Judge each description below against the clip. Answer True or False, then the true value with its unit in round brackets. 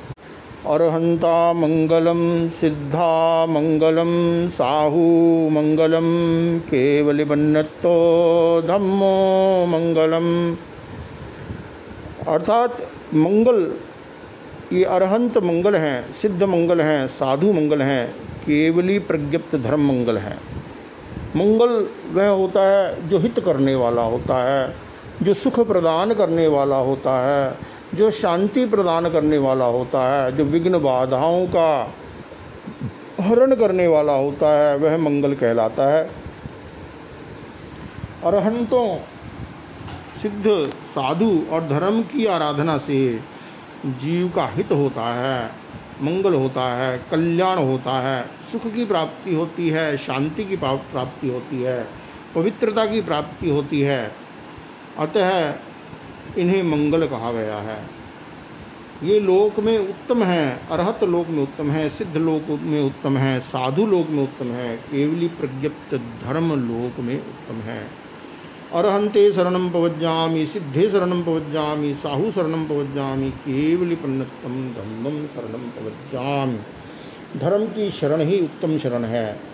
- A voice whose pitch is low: False (155 Hz)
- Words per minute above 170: False (115 wpm)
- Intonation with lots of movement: False (4.7 semitones)